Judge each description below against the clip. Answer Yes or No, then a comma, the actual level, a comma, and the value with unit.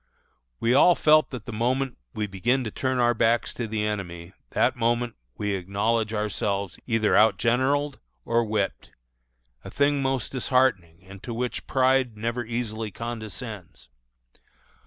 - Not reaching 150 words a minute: Yes, average, 140 wpm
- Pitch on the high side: No, low, 115 Hz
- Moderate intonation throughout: Yes, average, 3.3 semitones